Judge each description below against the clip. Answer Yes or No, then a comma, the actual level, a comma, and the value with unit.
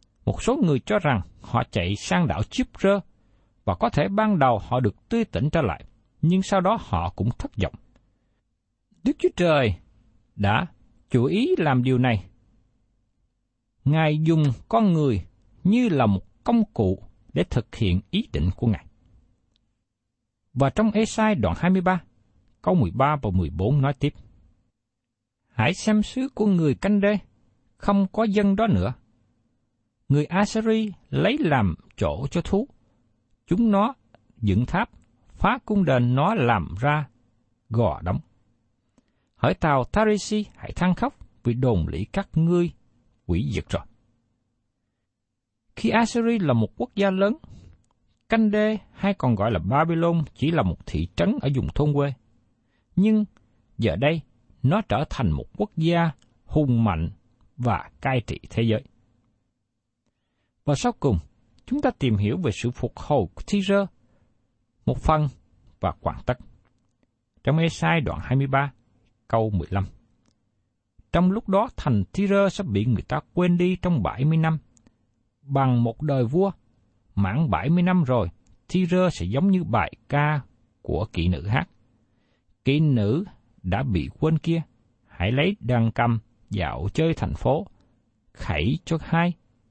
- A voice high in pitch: No, low, 120 Hz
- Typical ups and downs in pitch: No, wide, 7.4 semitones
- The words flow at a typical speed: No, slow, 150 wpm